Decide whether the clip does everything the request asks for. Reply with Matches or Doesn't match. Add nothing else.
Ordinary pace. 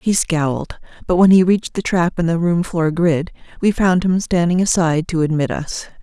Doesn't match